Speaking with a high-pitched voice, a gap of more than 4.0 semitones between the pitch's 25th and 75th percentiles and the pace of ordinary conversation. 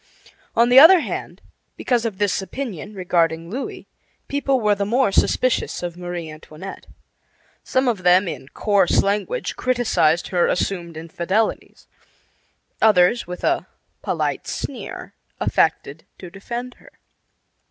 No: high, 195 Hz; wide, 5.4 semitones; slow, 125 wpm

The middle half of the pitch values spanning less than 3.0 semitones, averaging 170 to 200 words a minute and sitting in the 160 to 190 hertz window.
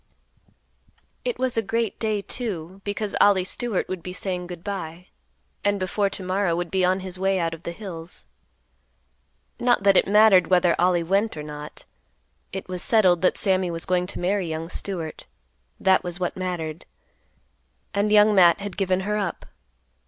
Yes: narrow, 2.5 semitones; average, 175 wpm; medium, 185 Hz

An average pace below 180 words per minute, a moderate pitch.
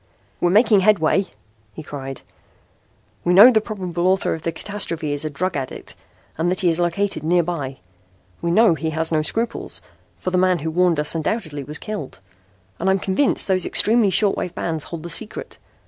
No: average, 185 wpm; medium, 175 Hz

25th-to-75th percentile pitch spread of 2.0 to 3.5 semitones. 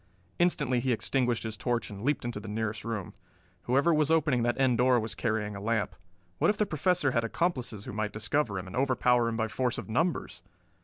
No: average, 4.0 semitones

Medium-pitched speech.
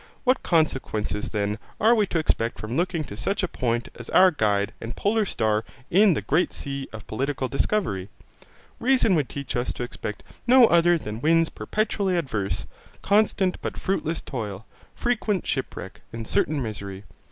Yes: medium, 145 Hz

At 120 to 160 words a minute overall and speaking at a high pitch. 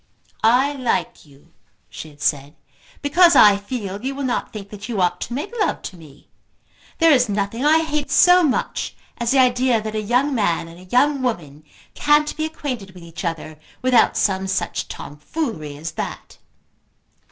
No: average, 180 wpm; high, 225 Hz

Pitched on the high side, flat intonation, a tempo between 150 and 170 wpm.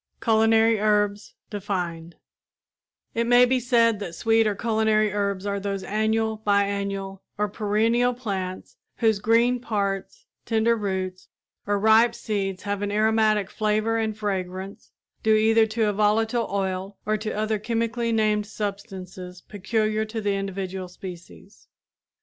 No: high, 210 Hz; narrow, 2.1 semitones; slow, 135 wpm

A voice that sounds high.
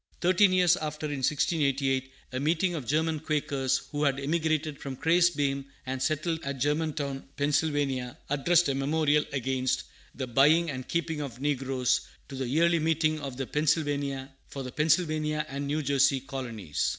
No: medium, 145 Hz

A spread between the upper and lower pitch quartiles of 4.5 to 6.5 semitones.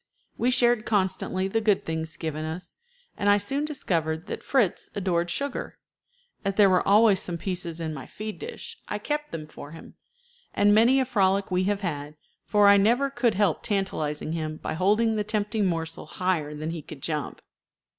Yes: average, 4.9 semitones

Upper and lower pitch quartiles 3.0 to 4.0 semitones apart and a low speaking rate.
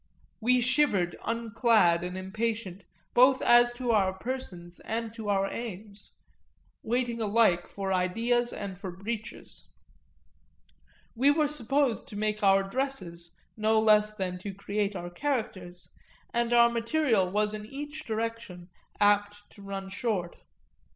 Yes: average, 3.6 semitones; slow, 130 wpm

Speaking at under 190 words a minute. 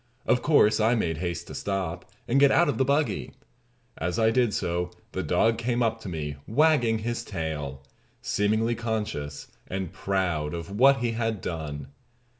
Yes: average, 170 wpm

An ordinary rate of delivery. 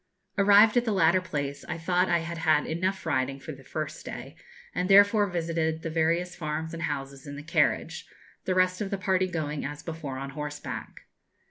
Yes: average, 195 wpm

